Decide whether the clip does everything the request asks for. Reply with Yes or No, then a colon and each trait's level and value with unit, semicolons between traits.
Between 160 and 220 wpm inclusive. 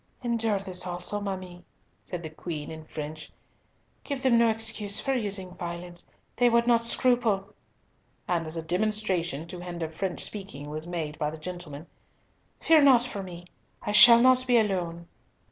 Yes: average, 165 wpm